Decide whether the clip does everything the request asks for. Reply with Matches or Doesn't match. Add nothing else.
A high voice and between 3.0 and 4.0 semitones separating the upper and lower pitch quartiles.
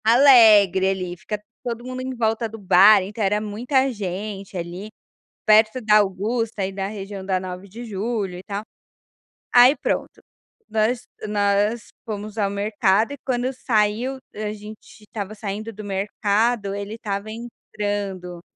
Doesn't match